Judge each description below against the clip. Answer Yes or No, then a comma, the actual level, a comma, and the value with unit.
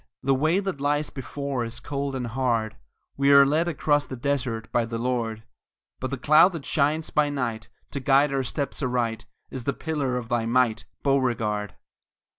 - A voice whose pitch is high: No, low, 135 Hz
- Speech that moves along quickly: No, average, 180 wpm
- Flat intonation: No, average, 3.3 semitones